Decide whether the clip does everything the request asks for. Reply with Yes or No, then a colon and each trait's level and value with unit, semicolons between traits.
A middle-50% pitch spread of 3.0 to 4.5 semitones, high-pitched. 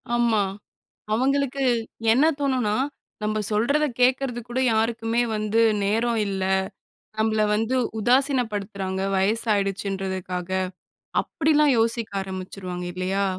Yes: average, 3.9 semitones; high, 220 Hz